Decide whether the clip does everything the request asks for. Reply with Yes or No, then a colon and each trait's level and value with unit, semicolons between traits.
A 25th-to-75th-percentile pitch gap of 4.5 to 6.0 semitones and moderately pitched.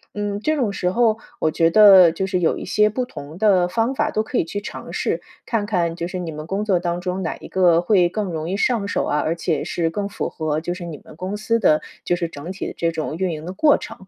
No: average, 3.8 semitones; medium, 180 Hz